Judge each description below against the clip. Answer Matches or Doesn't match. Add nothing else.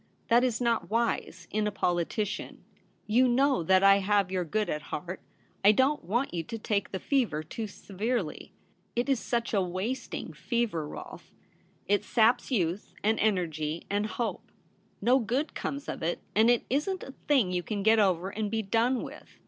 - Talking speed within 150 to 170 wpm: Doesn't match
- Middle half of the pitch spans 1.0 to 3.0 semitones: Doesn't match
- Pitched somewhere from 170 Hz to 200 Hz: Doesn't match